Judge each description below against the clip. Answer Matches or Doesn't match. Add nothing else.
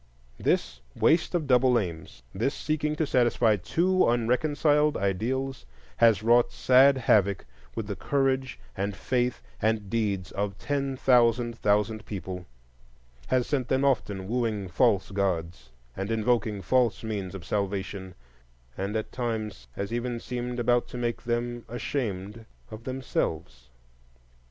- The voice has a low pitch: Matches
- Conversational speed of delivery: Doesn't match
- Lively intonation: Doesn't match